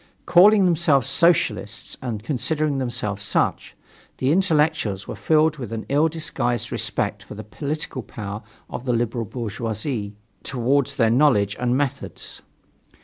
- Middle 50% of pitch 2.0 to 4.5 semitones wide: No, average, 5.3 semitones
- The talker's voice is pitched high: No, low, 130 Hz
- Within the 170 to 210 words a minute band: No, slow, 135 wpm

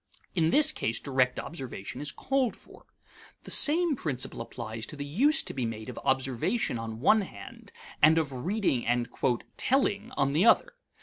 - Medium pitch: Yes, medium, 145 Hz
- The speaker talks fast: No, average, 170 wpm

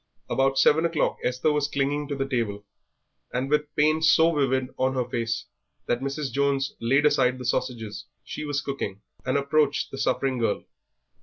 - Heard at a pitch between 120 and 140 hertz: Yes, low, 135 Hz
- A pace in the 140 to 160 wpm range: No, average, 170 wpm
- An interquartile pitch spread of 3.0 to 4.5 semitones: No, narrow, 2.6 semitones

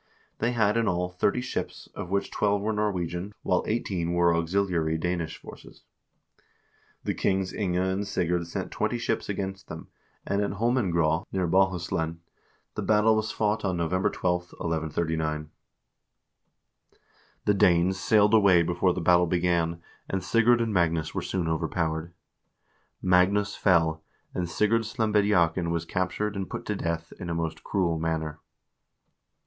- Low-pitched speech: Yes, very low, 90 Hz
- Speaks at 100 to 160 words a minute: Yes, average, 145 wpm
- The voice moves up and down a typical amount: Yes, average, 3.3 semitones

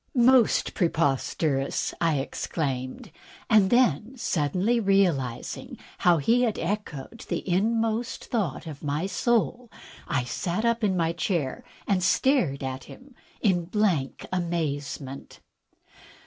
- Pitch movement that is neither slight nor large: No, wide, 7.6 semitones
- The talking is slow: Yes, slow, 115 wpm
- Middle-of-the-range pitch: Yes, medium, 180 Hz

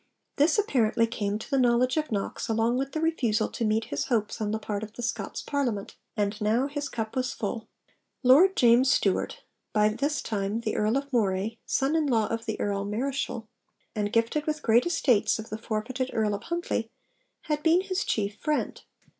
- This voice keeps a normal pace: Yes, average, 195 wpm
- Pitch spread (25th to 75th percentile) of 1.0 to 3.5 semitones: No, average, 4.5 semitones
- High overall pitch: Yes, high, 230 Hz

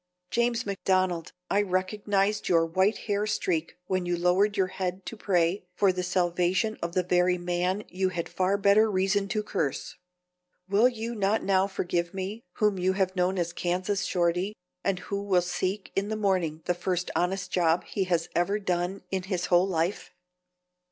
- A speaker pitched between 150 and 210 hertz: Yes, medium, 185 Hz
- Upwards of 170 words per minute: Yes, average, 180 wpm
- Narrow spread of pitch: Yes, narrow, 2.1 semitones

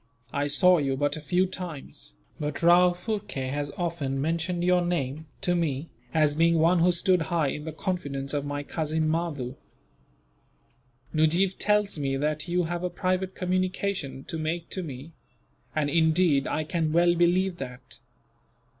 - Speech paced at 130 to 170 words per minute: Yes, average, 160 wpm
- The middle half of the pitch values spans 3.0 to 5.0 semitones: Yes, average, 3.6 semitones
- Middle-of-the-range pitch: Yes, medium, 165 Hz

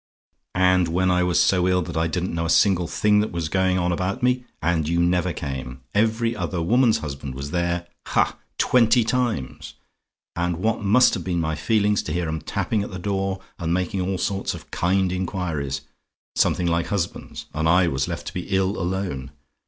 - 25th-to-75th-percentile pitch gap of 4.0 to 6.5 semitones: No, average, 2.8 semitones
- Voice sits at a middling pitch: No, very low, 90 Hz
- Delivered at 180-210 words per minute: Yes, average, 195 wpm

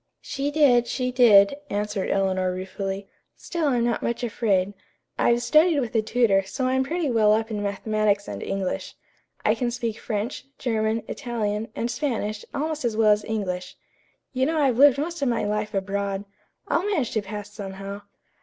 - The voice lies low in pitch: No, high, 220 Hz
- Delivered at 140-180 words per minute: Yes, average, 175 wpm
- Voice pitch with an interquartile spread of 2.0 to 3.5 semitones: No, average, 4.0 semitones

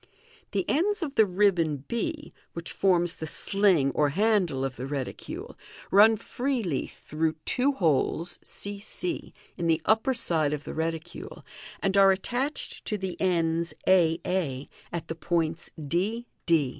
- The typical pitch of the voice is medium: Yes, medium, 175 Hz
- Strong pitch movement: No, average, 4.7 semitones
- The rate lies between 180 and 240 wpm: No, average, 150 wpm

